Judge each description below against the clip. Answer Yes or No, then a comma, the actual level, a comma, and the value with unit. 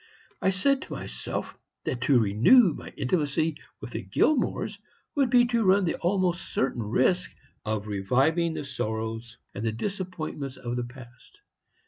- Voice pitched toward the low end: No, medium, 150 Hz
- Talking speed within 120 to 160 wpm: Yes, average, 150 wpm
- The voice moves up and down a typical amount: No, wide, 7.8 semitones